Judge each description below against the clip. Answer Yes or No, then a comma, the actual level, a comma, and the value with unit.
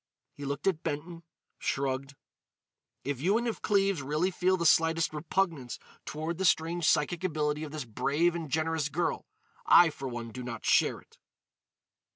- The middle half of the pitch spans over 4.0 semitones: No, average, 3.5 semitones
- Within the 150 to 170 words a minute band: Yes, average, 165 wpm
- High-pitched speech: No, medium, 155 Hz